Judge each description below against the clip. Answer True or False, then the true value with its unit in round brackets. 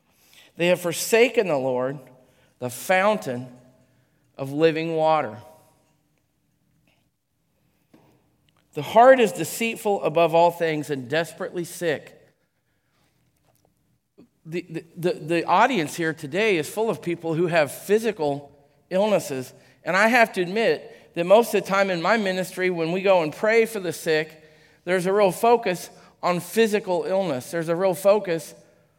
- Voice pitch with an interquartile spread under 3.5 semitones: False (4.1 semitones)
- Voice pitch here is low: False (170 Hz)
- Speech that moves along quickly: False (140 wpm)